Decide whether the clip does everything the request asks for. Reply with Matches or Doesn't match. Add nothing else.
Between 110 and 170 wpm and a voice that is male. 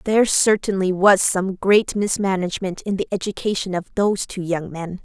Doesn't match